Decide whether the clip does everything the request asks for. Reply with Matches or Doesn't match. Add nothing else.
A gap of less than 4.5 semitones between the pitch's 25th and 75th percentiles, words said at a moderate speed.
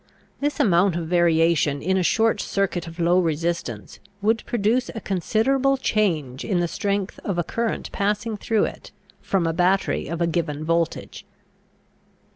Matches